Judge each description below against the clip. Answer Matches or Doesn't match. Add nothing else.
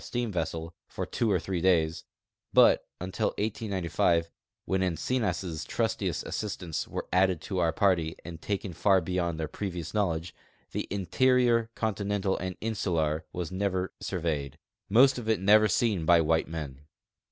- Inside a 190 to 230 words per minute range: Doesn't match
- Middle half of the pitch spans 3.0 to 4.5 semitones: Matches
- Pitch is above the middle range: Doesn't match